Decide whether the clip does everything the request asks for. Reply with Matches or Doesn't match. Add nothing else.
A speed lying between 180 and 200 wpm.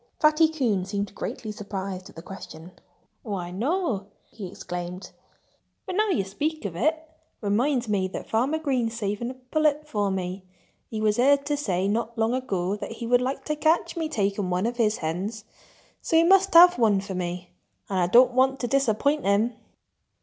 Matches